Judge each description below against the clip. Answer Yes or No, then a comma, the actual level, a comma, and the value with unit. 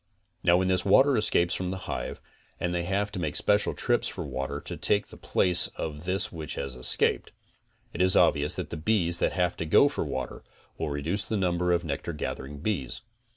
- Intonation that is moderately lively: Yes, average, 3.6 semitones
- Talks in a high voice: No, very low, 90 Hz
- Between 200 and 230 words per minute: Yes, fast, 205 wpm